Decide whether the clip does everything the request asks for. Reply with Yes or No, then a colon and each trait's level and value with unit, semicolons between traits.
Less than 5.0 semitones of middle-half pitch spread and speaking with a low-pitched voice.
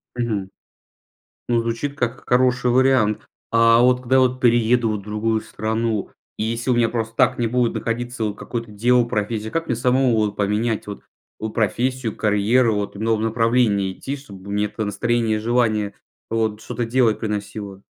Yes: narrow, 2.4 semitones; low, 115 Hz